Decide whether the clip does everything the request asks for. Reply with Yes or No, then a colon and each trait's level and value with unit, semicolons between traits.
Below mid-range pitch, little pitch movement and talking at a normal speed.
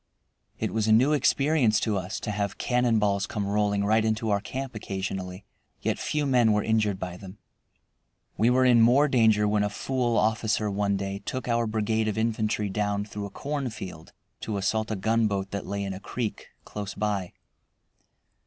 Yes: low, 105 Hz; narrow, 2.3 semitones; average, 180 wpm